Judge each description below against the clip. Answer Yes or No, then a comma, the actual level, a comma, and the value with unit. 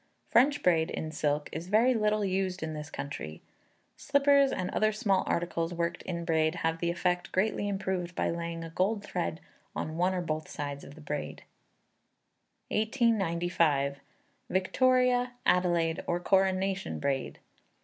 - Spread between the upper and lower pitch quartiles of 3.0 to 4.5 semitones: Yes, average, 4.0 semitones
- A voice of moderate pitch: Yes, medium, 175 Hz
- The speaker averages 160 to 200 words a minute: No, average, 145 wpm